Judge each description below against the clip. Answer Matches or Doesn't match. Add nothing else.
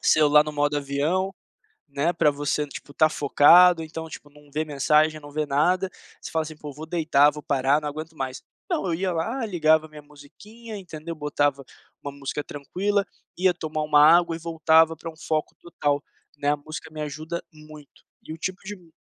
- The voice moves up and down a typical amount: Doesn't match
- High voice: Doesn't match